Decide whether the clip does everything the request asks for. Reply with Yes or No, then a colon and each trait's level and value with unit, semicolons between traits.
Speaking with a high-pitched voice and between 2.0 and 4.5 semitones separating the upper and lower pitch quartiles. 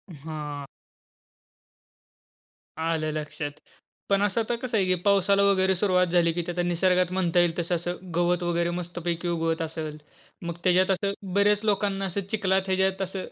No: medium, 180 Hz; narrow, 2.5 semitones